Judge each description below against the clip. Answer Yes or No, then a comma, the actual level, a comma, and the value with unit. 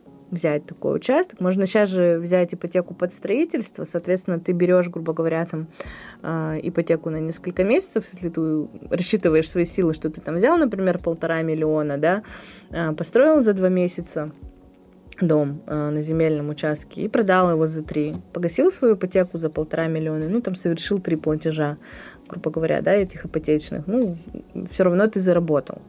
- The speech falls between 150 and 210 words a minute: Yes, average, 155 wpm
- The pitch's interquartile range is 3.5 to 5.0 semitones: No, average, 2.8 semitones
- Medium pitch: Yes, medium, 170 Hz